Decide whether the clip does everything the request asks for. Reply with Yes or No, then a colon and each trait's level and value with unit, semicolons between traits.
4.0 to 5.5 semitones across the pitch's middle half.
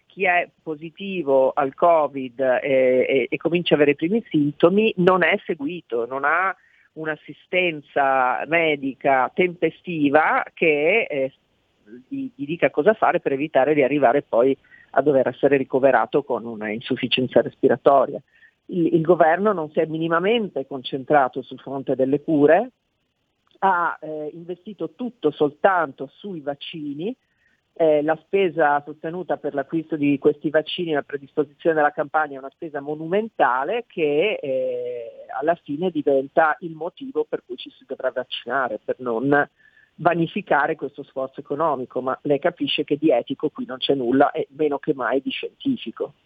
Yes: average, 4.5 semitones